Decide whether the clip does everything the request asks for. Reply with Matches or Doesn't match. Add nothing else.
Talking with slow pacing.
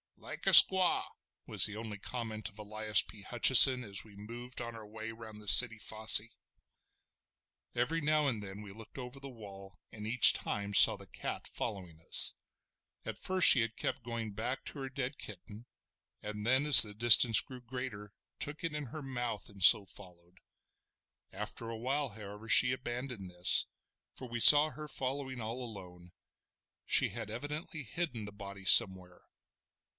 Doesn't match